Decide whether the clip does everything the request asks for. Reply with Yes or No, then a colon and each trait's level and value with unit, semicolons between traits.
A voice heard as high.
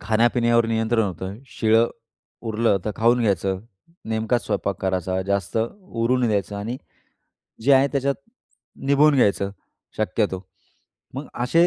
No: low, 115 Hz